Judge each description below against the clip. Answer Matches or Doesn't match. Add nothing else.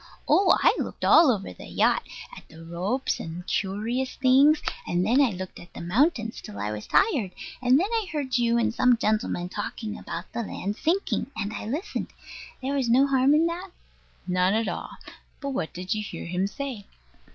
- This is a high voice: Matches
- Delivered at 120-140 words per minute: Doesn't match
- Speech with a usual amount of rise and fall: Doesn't match